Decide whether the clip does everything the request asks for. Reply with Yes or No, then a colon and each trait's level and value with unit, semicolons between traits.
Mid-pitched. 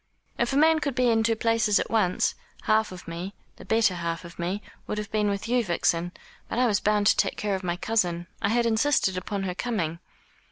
No: high, 210 Hz